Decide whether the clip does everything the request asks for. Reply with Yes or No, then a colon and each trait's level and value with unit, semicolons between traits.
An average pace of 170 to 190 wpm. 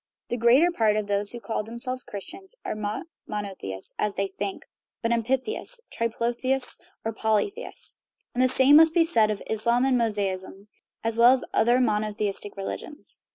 No: average, 155 wpm